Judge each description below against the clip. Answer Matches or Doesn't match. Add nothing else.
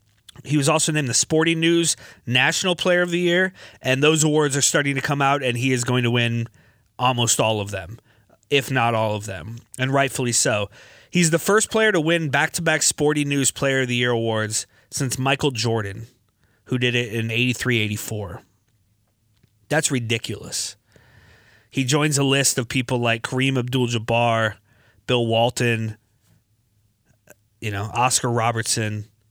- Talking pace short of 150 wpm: Doesn't match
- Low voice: Matches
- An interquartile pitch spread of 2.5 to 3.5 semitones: Doesn't match